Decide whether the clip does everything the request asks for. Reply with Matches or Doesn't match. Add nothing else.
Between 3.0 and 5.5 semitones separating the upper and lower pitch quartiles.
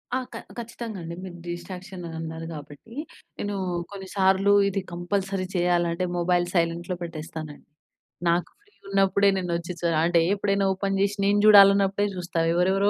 Doesn't match